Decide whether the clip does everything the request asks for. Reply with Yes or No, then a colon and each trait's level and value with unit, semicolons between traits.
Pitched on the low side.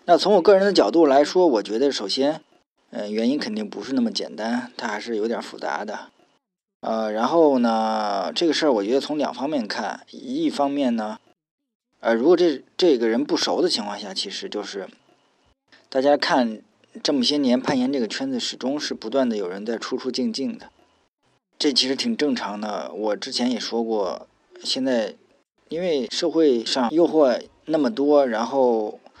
No: medium, 145 Hz